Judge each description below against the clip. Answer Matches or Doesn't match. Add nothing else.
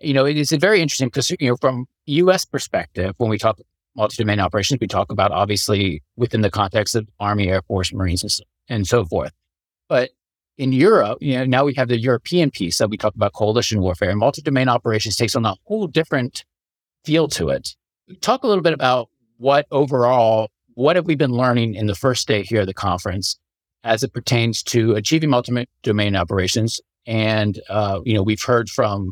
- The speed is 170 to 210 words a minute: Matches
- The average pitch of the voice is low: Matches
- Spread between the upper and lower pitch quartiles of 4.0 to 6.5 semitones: Matches